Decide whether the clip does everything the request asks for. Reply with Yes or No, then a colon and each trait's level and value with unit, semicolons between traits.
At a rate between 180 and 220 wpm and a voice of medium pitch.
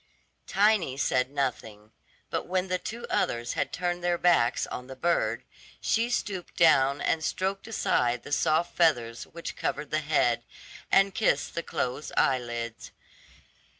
No: average, 145 wpm; medium, 155 Hz